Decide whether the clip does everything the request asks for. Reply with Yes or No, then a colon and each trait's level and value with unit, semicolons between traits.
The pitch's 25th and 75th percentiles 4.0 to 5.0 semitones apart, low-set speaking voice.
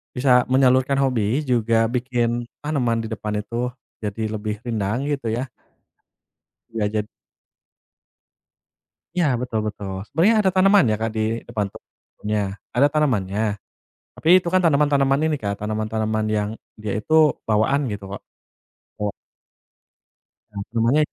Yes: average, 4.3 semitones; low, 115 Hz